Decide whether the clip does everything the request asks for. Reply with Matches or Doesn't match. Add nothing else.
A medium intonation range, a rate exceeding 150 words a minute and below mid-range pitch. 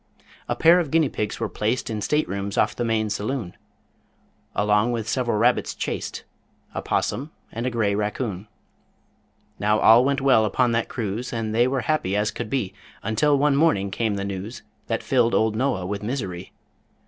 Matches